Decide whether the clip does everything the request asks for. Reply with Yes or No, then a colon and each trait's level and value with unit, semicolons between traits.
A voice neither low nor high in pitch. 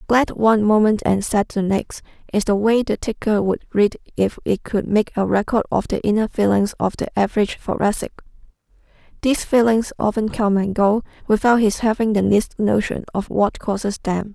No: high, 210 Hz